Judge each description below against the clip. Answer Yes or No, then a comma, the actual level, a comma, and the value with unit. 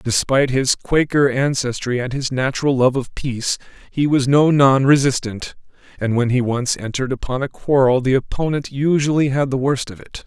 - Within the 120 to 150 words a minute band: No, average, 180 wpm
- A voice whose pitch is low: Yes, low, 130 Hz